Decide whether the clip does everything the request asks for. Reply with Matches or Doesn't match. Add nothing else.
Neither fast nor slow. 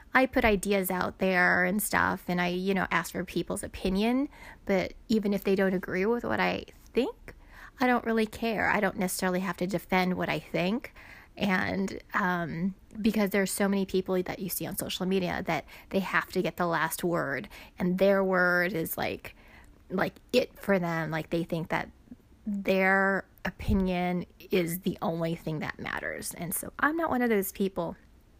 Matches